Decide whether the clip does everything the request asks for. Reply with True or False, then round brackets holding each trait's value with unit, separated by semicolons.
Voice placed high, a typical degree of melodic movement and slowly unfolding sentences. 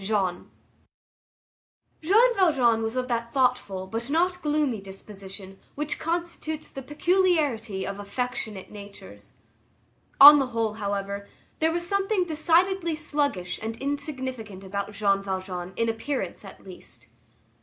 False (245 Hz; 7.4 semitones; 120 wpm)